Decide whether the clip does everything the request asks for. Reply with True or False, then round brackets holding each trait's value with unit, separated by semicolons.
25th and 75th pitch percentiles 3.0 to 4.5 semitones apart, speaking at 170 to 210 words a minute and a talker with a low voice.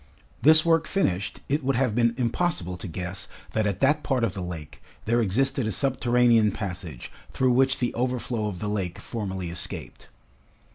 False (5.6 semitones; 175 wpm; 115 Hz)